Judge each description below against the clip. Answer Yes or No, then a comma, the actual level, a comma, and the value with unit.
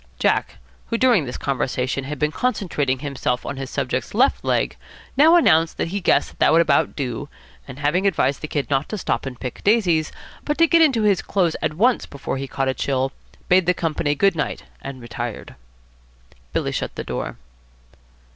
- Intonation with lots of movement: Yes, wide, 6.6 semitones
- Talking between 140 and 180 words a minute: No, average, 190 wpm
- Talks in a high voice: No, medium, 150 Hz